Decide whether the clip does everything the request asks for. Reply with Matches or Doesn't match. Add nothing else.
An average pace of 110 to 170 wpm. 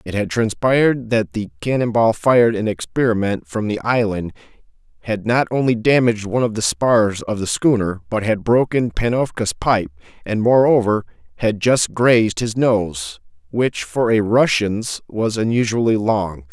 Matches